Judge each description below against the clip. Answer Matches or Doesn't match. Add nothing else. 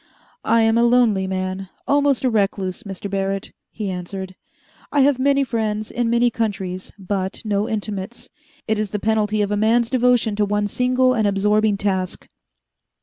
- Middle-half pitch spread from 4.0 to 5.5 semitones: Doesn't match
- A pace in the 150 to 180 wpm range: Matches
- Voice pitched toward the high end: Matches